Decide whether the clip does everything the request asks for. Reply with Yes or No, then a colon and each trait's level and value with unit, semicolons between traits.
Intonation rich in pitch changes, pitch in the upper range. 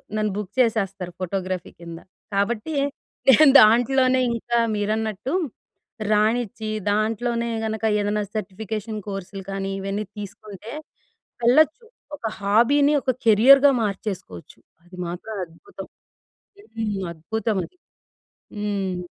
No: average, 3.1 semitones; high, 215 Hz